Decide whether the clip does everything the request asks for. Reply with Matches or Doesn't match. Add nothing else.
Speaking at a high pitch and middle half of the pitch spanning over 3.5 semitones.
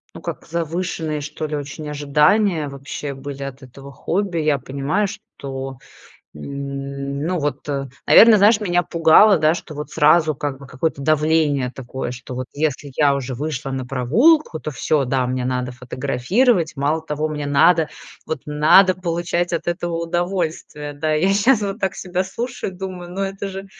Doesn't match